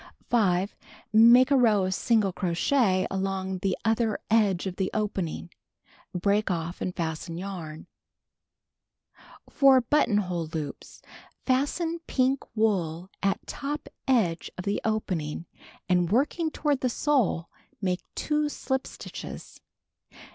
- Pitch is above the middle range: Yes, high, 200 Hz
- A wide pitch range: Yes, wide, 5.8 semitones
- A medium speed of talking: No, slow, 120 wpm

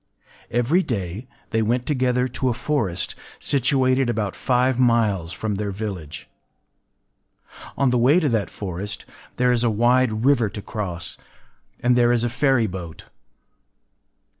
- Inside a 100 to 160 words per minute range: Yes, average, 140 wpm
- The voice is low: Yes, low, 120 Hz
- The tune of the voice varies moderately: Yes, average, 3.7 semitones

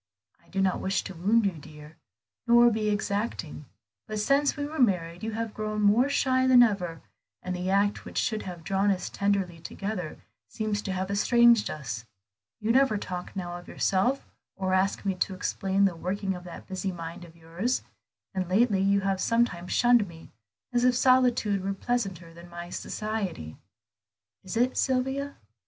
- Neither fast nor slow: Yes, average, 175 wpm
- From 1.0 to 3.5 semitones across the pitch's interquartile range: No, average, 4.4 semitones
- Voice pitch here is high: Yes, high, 195 Hz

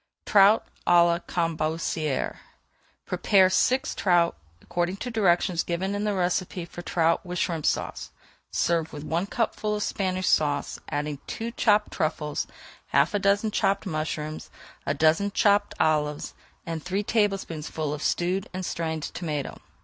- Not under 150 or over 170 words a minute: No, average, 140 wpm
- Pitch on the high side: No, medium, 175 Hz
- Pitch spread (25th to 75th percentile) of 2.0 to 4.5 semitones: Yes, average, 3.9 semitones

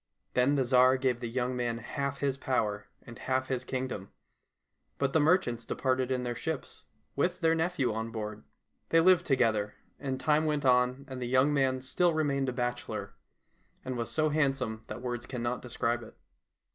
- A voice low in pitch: Yes, low, 130 Hz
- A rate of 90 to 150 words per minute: No, average, 180 wpm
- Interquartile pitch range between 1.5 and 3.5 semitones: Yes, narrow, 2.6 semitones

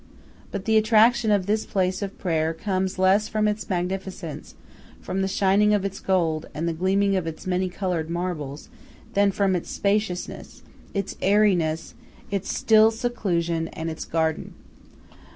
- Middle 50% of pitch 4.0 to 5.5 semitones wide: No, average, 3.3 semitones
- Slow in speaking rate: No, average, 150 wpm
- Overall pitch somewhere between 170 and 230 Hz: Yes, high, 190 Hz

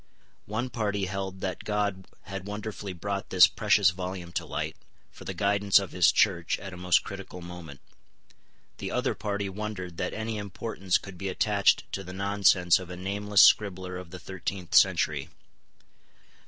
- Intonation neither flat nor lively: No, narrow, 2.0 semitones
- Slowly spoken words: No, average, 165 wpm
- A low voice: Yes, very low, 95 Hz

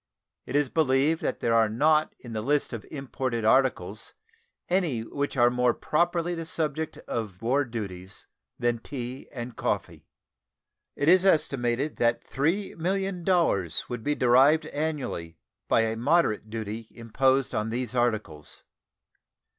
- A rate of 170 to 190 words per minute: No, slow, 135 wpm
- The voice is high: No, low, 130 Hz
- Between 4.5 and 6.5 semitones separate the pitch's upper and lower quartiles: Yes, average, 5.1 semitones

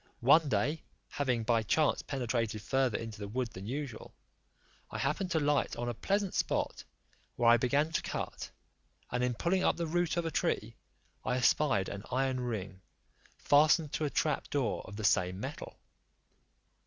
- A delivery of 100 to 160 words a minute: No, average, 170 wpm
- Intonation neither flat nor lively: Yes, average, 4.9 semitones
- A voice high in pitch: No, low, 130 Hz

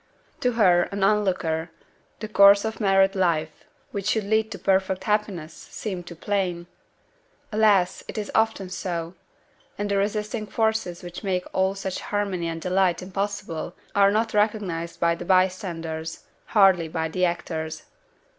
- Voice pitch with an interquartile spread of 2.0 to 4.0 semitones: Yes, average, 3.1 semitones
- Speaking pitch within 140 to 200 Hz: Yes, high, 190 Hz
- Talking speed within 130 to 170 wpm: Yes, average, 150 wpm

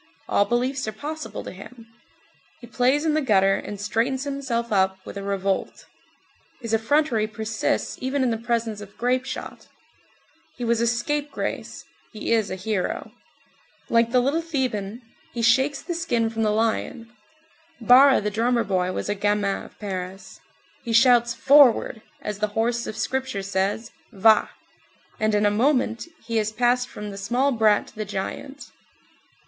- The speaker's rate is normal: Yes, average, 165 wpm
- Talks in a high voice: Yes, high, 230 Hz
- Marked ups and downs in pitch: No, average, 3.3 semitones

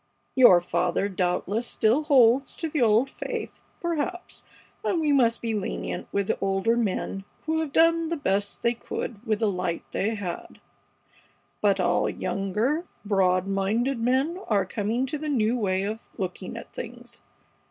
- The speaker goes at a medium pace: Yes, average, 160 wpm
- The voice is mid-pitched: No, high, 225 Hz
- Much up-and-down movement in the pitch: Yes, wide, 5.9 semitones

